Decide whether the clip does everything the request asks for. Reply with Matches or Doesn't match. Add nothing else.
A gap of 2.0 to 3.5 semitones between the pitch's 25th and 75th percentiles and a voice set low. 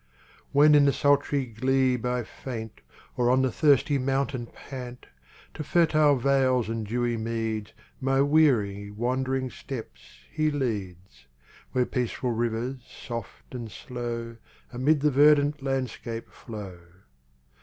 Matches